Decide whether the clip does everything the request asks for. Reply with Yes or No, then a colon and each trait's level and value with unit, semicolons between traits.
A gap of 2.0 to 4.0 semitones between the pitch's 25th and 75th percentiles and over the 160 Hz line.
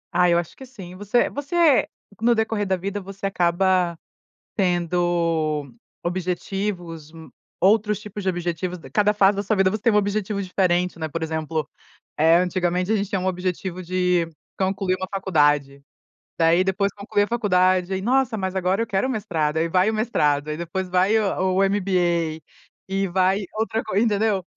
Yes: average, 2.8 semitones; medium, 185 Hz